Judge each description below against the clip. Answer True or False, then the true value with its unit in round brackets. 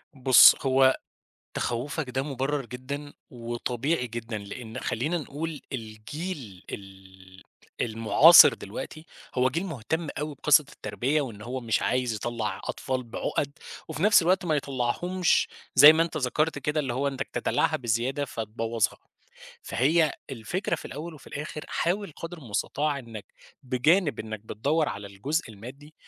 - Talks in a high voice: False (130 Hz)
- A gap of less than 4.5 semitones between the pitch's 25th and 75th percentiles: False (4.8 semitones)